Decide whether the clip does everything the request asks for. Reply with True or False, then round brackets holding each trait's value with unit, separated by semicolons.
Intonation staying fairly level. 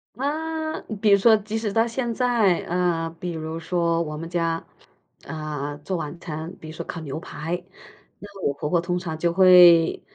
False (4.0 semitones)